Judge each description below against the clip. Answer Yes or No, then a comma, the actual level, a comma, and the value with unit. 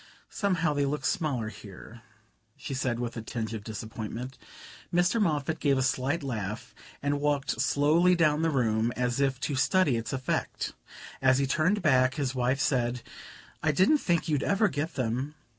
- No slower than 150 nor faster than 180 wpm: Yes, average, 170 wpm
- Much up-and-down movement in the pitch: No, average, 4.2 semitones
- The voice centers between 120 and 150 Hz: Yes, low, 135 Hz